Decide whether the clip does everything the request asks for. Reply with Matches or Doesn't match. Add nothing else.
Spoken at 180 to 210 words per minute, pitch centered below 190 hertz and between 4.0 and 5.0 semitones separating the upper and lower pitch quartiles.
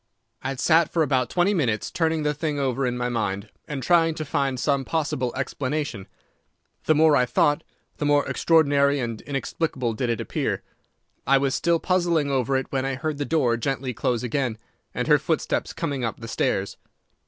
Doesn't match